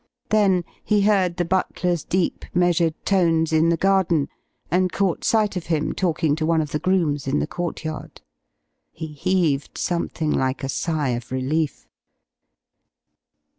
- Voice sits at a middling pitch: Yes, medium, 165 Hz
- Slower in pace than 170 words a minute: Yes, average, 145 wpm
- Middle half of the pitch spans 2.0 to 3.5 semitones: Yes, average, 3.2 semitones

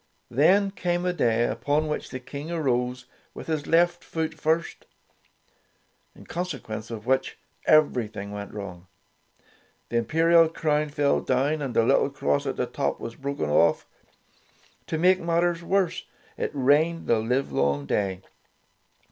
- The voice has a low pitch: No, medium, 145 Hz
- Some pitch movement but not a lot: No, wide, 6.2 semitones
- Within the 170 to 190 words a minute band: No, average, 150 wpm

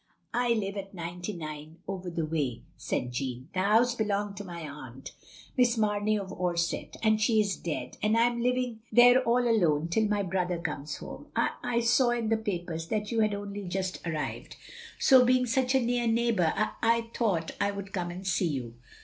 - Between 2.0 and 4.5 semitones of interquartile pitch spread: No, average, 5.3 semitones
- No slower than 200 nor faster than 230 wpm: Yes, fast, 205 wpm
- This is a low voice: No, high, 200 Hz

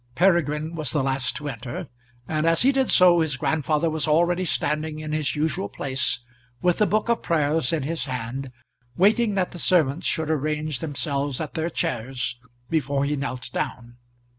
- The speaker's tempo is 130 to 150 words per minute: No, average, 175 wpm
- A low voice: No, medium, 155 Hz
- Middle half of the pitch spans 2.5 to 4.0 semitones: Yes, average, 3.5 semitones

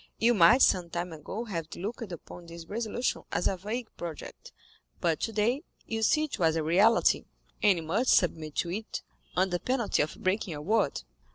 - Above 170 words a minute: Yes, average, 180 wpm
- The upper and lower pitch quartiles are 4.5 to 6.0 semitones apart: Yes, average, 5.0 semitones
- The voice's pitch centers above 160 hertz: Yes, high, 190 Hz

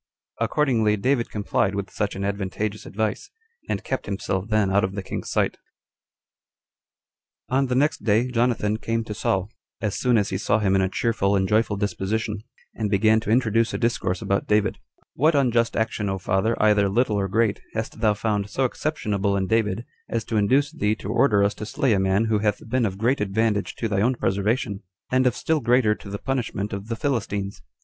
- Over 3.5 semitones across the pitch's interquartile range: No, narrow, 2.6 semitones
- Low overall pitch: Yes, low, 110 Hz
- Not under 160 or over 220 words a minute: Yes, average, 200 wpm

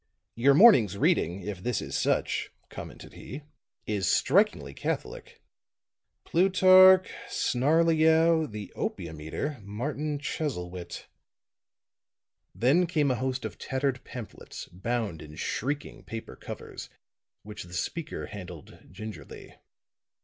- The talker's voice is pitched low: Yes, low, 125 Hz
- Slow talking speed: Yes, slow, 105 wpm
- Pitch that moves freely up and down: Yes, wide, 7.8 semitones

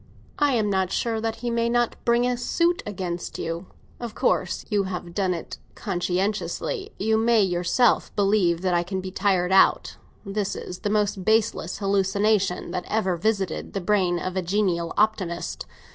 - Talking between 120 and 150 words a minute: No, average, 170 wpm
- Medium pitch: No, high, 195 Hz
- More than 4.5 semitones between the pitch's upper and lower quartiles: No, average, 3.5 semitones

